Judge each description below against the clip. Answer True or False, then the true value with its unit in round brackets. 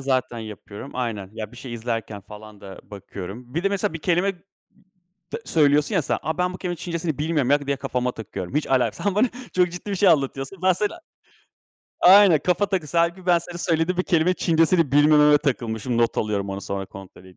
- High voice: False (145 Hz)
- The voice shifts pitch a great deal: True (7.6 semitones)